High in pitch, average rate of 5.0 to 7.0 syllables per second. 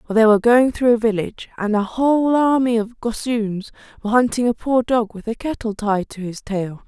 Yes: high, 230 Hz; 5.4 syllables/s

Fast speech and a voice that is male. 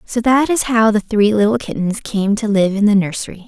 No: fast, 240 wpm; female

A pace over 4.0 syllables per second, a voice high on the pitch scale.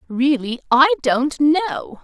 No: 3.0 syllables/s; very high, 285 Hz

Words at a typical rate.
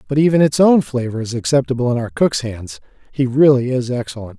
Yes: average, 190 wpm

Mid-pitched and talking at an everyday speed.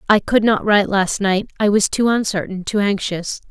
No: high, 205 Hz; average, 190 wpm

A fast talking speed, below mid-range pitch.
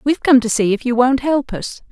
No: fast, 280 wpm; very high, 250 Hz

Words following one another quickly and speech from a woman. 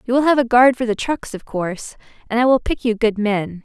Yes: fast, 280 wpm; female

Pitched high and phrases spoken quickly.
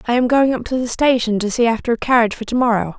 Yes: high, 235 Hz; fast, 300 wpm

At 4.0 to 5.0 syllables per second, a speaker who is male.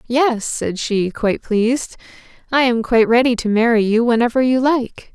No: 4.9 syllables/s; female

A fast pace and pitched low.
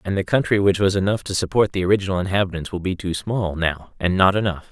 Yes: fast, 240 wpm; very low, 95 Hz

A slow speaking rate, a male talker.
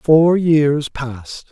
Yes: slow, 120 wpm; male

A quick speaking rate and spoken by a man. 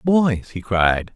No: average, 155 wpm; male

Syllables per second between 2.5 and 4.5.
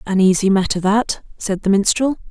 No: 5.1 syllables/s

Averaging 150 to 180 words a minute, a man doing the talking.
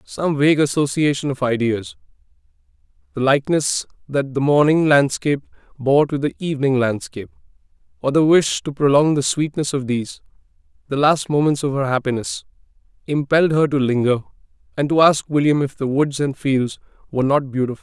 Yes: average, 155 wpm; male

